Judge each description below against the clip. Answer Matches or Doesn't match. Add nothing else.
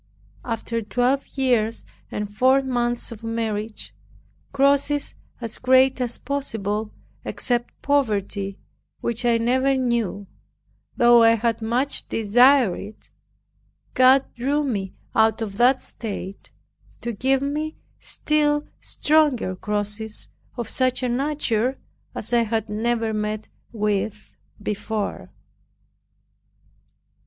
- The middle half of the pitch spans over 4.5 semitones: Doesn't match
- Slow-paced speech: Matches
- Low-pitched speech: Doesn't match